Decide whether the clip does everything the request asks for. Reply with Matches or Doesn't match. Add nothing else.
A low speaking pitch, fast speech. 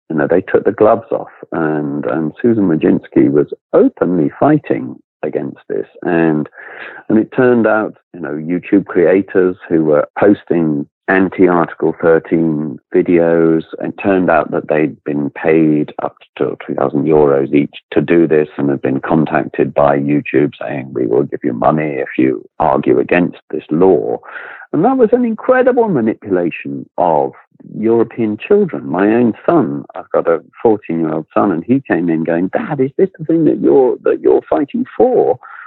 Doesn't match